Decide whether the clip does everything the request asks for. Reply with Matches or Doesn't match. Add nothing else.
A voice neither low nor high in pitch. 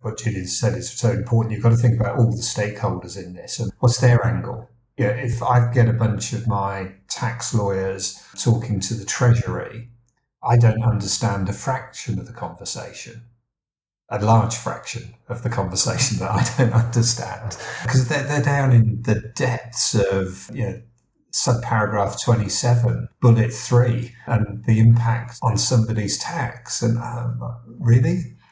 Doesn't match